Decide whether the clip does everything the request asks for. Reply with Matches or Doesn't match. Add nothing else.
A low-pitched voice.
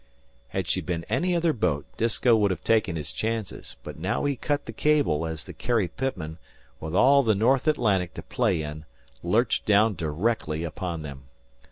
Matches